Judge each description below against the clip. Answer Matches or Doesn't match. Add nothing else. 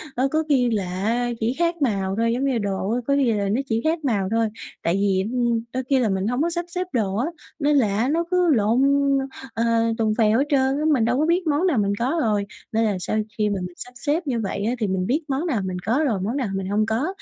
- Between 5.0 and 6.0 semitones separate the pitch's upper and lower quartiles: Matches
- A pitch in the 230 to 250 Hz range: Matches